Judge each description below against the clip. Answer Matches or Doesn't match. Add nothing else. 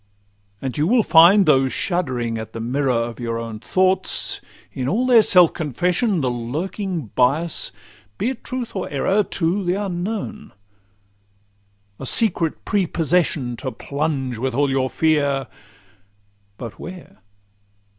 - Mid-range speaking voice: Matches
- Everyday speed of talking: Doesn't match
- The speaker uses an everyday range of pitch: Doesn't match